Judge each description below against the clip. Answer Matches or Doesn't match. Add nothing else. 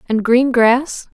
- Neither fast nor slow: Matches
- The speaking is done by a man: Doesn't match